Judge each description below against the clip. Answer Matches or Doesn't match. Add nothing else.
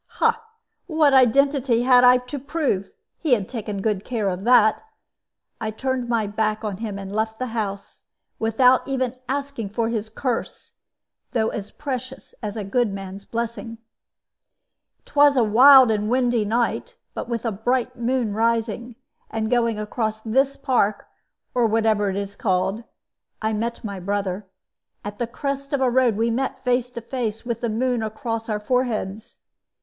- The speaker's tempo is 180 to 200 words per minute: Doesn't match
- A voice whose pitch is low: Doesn't match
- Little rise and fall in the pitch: Doesn't match